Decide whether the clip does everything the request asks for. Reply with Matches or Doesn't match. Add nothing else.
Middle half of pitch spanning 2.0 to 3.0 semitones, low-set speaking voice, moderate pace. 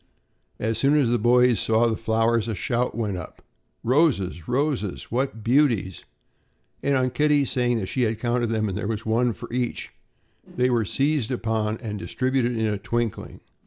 Matches